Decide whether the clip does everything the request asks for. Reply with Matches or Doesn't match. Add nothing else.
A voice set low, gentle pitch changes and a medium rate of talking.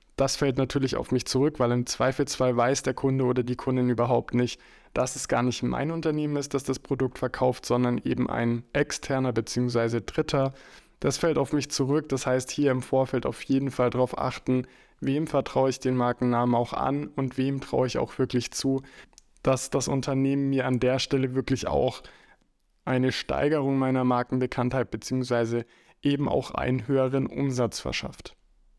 Matches